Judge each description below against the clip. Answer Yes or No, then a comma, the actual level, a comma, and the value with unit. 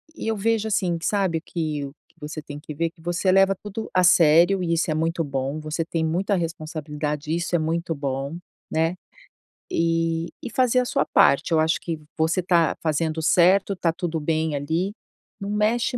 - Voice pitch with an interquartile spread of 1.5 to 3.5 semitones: Yes, average, 2.9 semitones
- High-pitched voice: No, medium, 165 Hz